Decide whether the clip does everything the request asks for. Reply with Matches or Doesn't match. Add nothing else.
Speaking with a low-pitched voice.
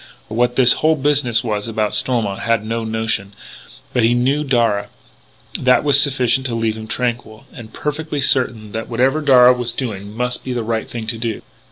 Matches